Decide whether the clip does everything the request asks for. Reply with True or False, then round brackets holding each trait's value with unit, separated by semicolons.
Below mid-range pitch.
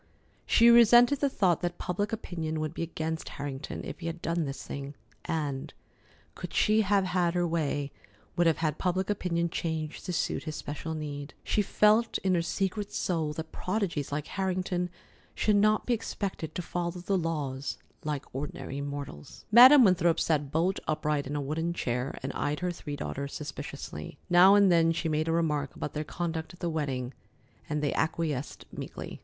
False (165 Hz)